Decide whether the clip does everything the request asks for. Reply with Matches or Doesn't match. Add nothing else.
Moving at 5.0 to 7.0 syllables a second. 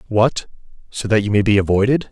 Matches